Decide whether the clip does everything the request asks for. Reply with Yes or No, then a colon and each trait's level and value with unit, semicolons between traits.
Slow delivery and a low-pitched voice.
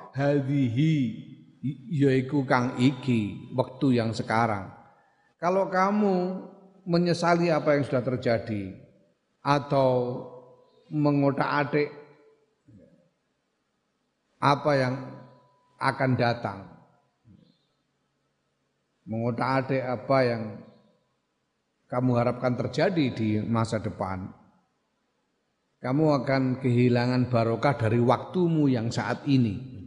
Yes: slow, 80 wpm; low, 130 Hz